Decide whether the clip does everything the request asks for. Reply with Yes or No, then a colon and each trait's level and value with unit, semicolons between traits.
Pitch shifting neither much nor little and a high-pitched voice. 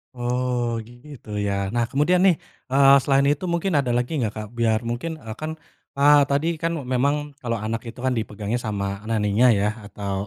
No: average, 4.6 semitones; low, 120 Hz